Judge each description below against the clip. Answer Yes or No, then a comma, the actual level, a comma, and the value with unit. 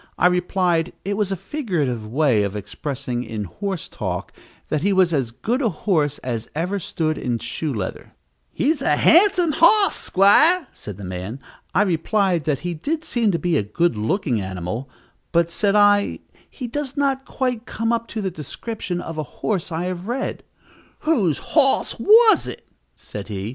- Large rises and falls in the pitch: Yes, wide, 8.7 semitones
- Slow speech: No, average, 175 wpm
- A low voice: No, medium, 180 Hz